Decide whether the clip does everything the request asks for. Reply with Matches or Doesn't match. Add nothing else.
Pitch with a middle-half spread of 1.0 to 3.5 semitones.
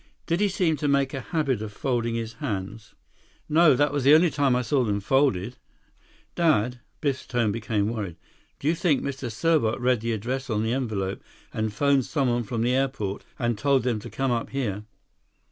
Doesn't match